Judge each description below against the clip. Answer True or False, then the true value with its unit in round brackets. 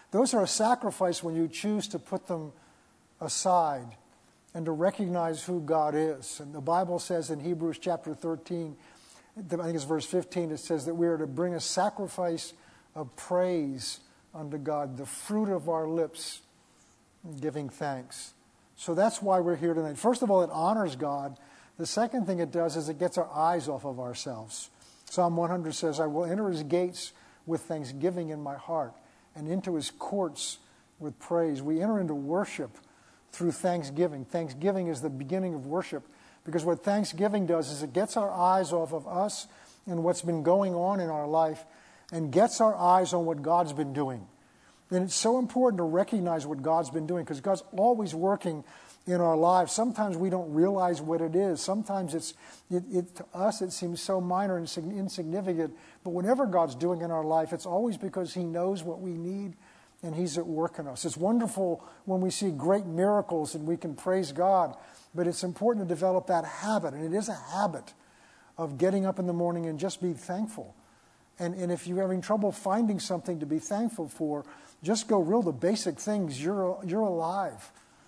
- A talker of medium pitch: True (175 Hz)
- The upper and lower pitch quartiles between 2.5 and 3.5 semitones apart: True (2.8 semitones)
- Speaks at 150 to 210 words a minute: True (190 wpm)